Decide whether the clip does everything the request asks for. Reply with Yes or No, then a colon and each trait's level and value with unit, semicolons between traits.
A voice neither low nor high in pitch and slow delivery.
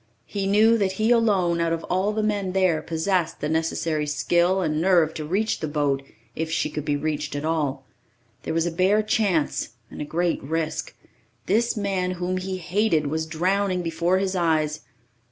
No: medium, 175 Hz; average, 185 wpm